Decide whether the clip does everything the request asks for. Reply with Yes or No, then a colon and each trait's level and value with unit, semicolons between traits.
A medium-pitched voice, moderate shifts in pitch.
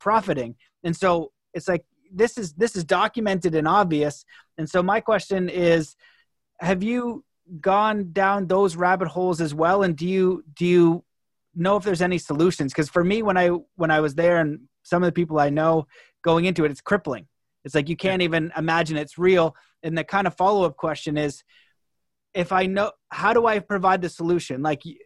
Yes: medium, 175 Hz; average, 3.3 semitones